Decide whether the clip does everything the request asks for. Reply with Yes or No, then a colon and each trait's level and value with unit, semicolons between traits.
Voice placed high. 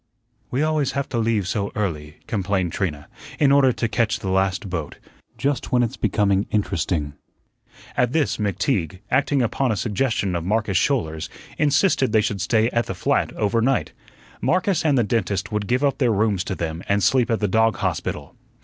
No: low, 110 Hz